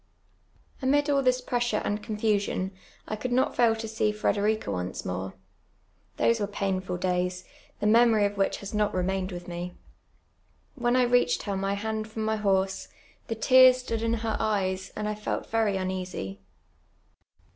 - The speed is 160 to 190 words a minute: Yes, average, 165 wpm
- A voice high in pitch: Yes, high, 210 Hz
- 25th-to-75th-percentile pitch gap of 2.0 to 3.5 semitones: Yes, average, 3.2 semitones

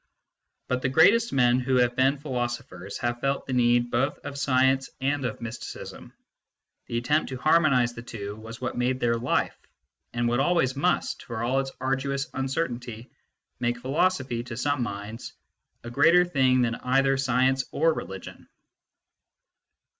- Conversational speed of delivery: Yes, average, 155 wpm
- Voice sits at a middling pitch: No, low, 130 Hz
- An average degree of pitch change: No, narrow, 2.3 semitones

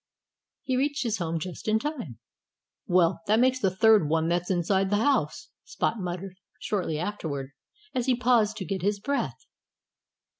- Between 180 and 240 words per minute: No, average, 160 wpm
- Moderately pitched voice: No, high, 200 Hz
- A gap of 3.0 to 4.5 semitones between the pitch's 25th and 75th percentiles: No, average, 5.2 semitones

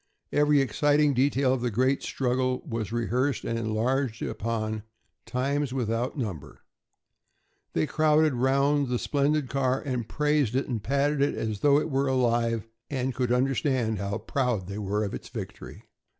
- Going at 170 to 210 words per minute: No, average, 155 wpm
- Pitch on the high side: No, low, 130 Hz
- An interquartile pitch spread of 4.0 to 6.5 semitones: No, average, 3.4 semitones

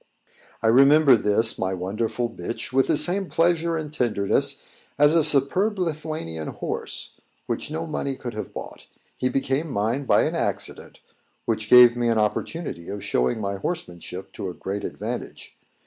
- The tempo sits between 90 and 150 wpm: No, average, 160 wpm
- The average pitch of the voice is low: Yes, low, 125 Hz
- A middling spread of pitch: No, wide, 7.0 semitones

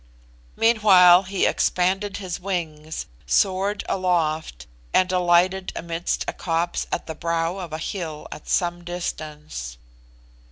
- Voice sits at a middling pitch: Yes, medium, 175 Hz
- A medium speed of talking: No, slow, 120 wpm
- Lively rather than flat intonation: No, narrow, 2.6 semitones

